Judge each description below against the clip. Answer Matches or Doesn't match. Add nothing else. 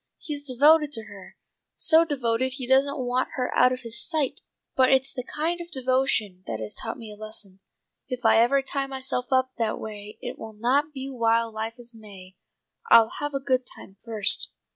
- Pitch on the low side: Doesn't match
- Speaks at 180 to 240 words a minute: Matches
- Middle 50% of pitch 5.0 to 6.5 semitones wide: Doesn't match